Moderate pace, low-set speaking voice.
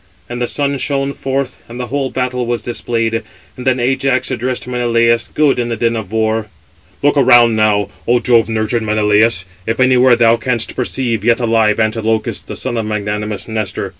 Yes: average, 180 wpm; low, 120 Hz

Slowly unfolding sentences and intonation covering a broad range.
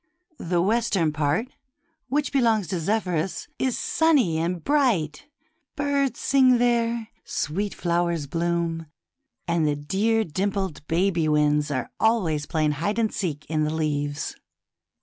Yes: slow, 130 wpm; wide, 6.6 semitones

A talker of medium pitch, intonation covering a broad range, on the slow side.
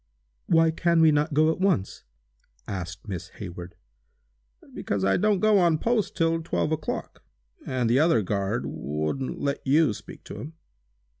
No: medium, 145 Hz; wide, 8.7 semitones; average, 155 wpm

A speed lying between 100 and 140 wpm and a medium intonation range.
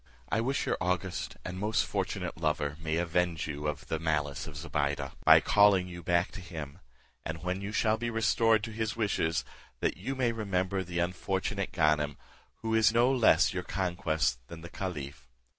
No: average, 180 wpm; average, 4.8 semitones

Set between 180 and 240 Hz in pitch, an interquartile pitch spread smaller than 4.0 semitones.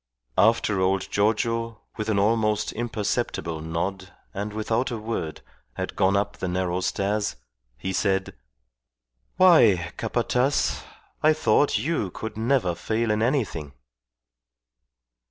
No: low, 105 Hz; average, 3.4 semitones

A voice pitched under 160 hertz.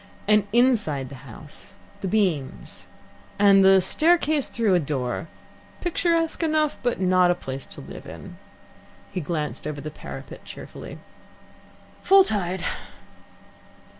No: high, 190 Hz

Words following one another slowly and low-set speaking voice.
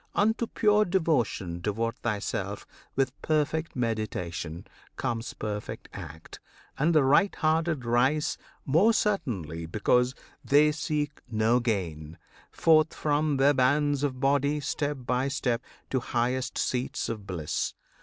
Yes: slow, 125 wpm; low, 130 Hz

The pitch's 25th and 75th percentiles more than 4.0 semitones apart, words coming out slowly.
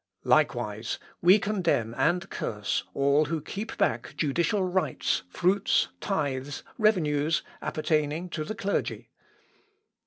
Yes: average, 4.9 semitones; slow, 115 wpm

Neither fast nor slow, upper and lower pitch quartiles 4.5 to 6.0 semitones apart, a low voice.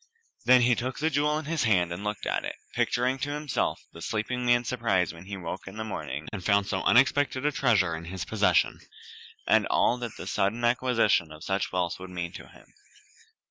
No: fast, 210 wpm; average, 5.3 semitones; low, 110 Hz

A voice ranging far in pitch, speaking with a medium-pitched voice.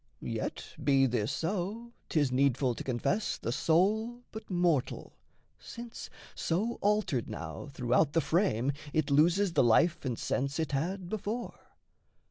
Yes: wide, 7.2 semitones; medium, 165 Hz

